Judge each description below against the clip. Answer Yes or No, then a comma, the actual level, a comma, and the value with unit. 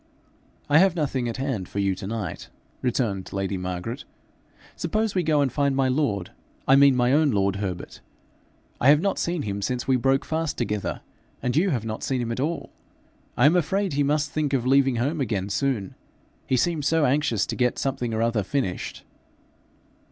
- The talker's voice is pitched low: Yes, low, 130 Hz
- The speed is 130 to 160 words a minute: No, average, 190 wpm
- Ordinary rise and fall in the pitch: Yes, average, 4.9 semitones